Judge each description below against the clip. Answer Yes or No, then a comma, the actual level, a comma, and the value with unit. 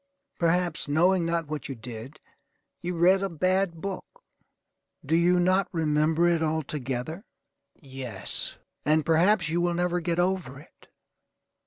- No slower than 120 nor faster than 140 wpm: Yes, slow, 135 wpm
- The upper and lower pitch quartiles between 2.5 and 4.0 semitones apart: Yes, average, 2.9 semitones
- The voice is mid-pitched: Yes, medium, 165 Hz